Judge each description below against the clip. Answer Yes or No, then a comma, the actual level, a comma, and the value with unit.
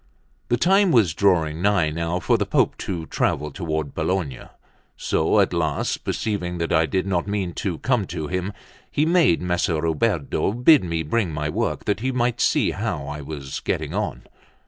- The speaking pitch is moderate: No, very low, 90 Hz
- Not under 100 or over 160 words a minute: No, average, 180 wpm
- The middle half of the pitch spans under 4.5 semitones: No, average, 4.8 semitones